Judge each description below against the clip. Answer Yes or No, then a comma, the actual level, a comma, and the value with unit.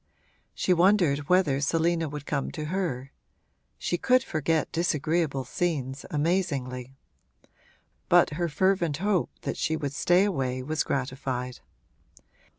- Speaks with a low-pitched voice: No, medium, 155 Hz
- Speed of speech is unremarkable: No, slow, 120 wpm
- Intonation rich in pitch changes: No, average, 4.4 semitones